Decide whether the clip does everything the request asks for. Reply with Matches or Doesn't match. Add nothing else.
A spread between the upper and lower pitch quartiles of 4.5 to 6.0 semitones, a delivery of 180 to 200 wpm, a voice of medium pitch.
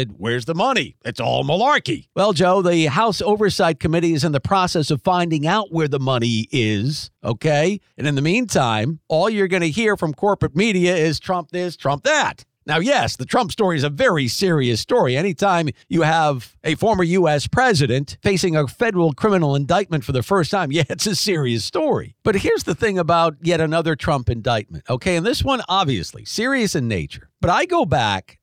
Matches